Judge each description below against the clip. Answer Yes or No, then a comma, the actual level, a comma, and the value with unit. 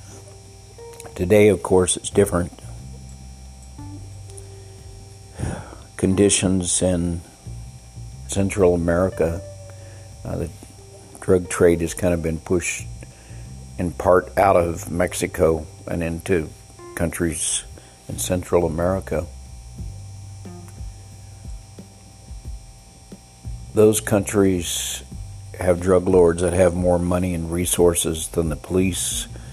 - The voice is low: Yes, very low, 90 Hz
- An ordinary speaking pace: No, slow, 85 wpm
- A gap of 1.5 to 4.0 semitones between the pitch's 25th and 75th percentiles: Yes, average, 2.9 semitones